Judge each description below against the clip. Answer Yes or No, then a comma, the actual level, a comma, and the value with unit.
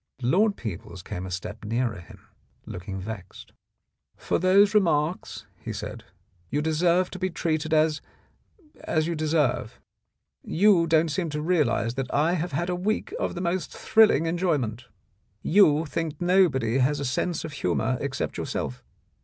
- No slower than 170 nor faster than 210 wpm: No, average, 160 wpm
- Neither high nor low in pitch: Yes, medium, 155 Hz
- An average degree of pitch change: No, wide, 6.1 semitones